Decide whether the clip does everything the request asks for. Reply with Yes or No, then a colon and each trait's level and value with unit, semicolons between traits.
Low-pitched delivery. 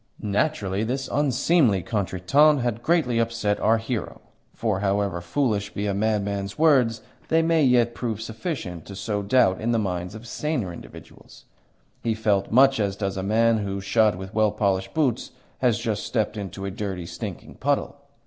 Yes: low, 110 Hz